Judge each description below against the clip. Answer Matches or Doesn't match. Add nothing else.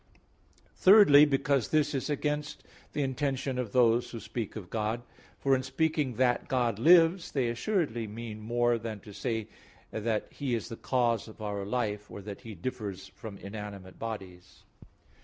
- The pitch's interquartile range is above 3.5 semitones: Matches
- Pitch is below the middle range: Matches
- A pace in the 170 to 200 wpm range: Doesn't match